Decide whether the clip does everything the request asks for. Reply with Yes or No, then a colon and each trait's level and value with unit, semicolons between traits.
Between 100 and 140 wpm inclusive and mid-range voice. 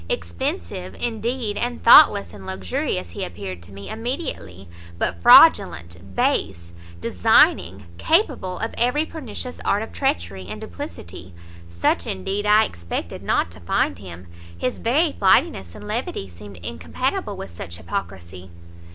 No: slow, 135 wpm; very low, 95 Hz